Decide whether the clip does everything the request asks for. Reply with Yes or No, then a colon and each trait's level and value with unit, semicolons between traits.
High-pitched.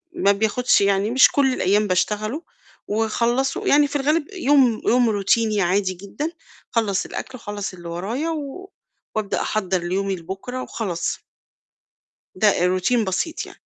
Yes: high, 215 Hz